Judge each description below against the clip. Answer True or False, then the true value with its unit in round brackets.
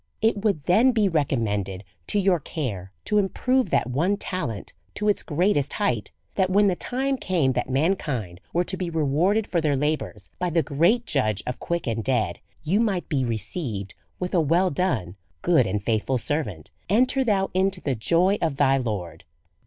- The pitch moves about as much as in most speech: False (7.5 semitones)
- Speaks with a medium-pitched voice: True (160 Hz)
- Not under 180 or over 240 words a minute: True (185 wpm)